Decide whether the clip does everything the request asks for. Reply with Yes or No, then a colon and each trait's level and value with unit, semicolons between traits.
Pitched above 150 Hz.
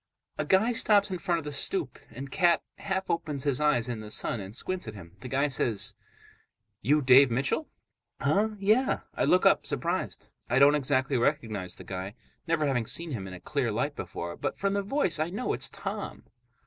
No: medium, 145 Hz